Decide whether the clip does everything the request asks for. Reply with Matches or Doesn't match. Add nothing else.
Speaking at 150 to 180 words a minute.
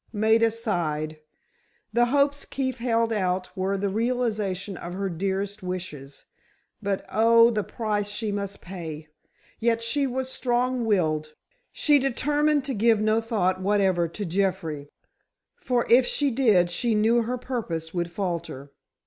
Doesn't match